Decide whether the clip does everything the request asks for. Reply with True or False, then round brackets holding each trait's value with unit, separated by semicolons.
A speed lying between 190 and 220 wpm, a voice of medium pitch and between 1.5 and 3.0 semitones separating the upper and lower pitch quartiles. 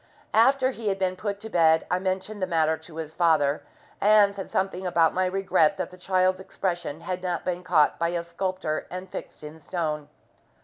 True (195 wpm; 180 Hz; 2.7 semitones)